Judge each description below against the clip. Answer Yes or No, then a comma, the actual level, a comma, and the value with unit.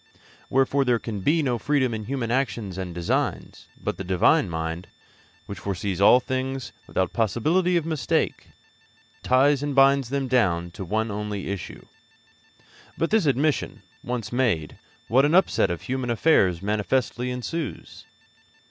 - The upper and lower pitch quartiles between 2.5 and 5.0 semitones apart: No, wide, 5.4 semitones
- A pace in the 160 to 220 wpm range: No, average, 145 wpm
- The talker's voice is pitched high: No, low, 120 Hz